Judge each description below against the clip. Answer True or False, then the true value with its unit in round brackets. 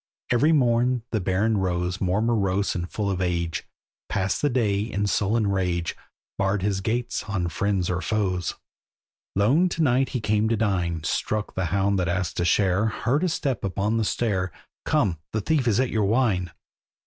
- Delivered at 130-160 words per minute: False (180 wpm)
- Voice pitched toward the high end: False (100 Hz)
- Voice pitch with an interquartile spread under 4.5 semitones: True (3.8 semitones)